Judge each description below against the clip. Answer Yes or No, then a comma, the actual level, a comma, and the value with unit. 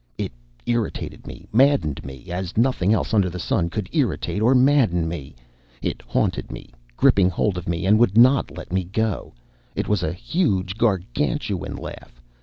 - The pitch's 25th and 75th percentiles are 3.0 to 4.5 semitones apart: No, average, 5.1 semitones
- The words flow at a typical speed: Yes, average, 170 wpm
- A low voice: Yes, low, 100 Hz